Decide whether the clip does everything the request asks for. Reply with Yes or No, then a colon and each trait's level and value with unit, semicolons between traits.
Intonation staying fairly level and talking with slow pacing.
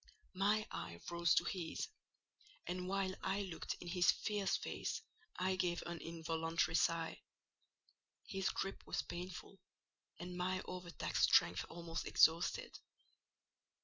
Yes: narrow, 2.2 semitones; slow, 125 wpm